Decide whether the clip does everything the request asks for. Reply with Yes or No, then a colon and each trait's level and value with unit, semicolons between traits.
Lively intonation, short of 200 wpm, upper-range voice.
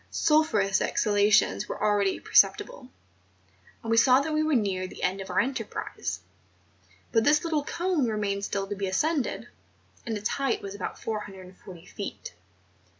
Yes: wide, 6.0 semitones; average, 155 wpm; high, 210 Hz